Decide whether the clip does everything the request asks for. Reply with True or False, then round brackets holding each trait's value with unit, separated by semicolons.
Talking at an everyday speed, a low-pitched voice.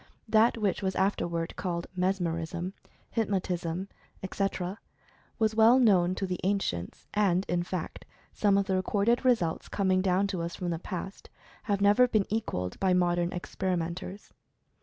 False (160 wpm; 190 Hz)